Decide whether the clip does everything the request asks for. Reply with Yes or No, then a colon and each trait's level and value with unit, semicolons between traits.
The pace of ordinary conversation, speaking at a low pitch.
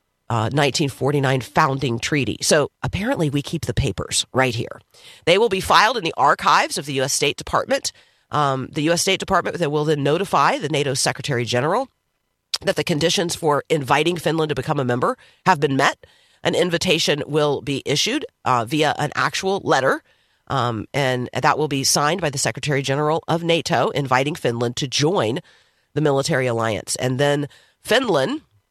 No: average, 170 wpm; medium, 145 Hz